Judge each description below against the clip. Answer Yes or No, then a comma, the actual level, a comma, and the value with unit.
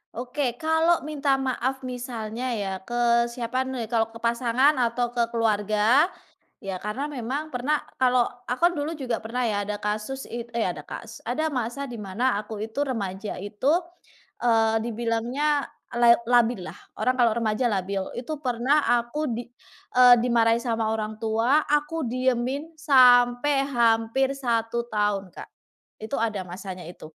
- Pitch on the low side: No, high, 240 Hz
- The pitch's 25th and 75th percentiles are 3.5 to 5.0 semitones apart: No, average, 2.8 semitones